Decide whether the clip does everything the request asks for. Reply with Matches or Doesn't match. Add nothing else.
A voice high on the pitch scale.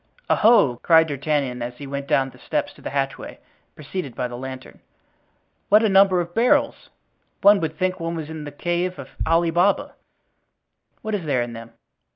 Doesn't match